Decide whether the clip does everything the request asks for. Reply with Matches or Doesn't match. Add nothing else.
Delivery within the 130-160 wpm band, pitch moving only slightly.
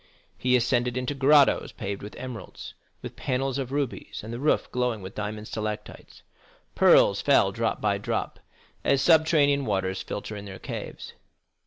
Doesn't match